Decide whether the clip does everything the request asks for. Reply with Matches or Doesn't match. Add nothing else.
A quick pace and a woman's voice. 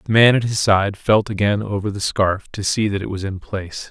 Doesn't match